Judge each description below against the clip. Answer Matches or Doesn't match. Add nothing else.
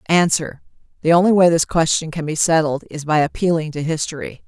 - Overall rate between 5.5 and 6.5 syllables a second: Matches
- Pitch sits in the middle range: Matches